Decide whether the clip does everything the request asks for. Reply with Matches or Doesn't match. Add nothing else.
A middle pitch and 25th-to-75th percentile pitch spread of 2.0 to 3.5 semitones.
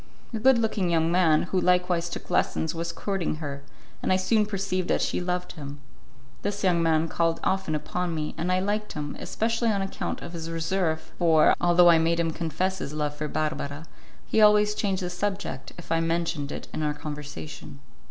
Matches